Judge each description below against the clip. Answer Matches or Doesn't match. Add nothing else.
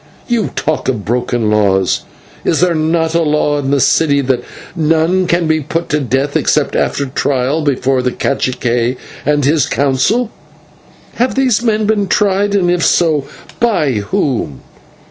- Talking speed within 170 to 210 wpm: Doesn't match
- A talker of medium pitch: Matches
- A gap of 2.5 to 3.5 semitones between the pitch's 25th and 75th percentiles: Doesn't match